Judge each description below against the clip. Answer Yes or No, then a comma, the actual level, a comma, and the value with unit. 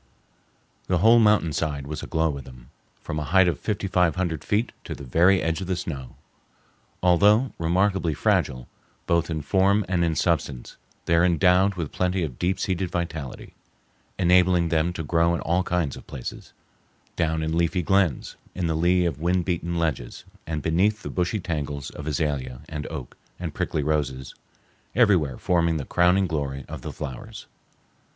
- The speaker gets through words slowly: No, average, 165 wpm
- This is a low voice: Yes, very low, 85 Hz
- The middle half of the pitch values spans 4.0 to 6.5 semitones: No, average, 3.3 semitones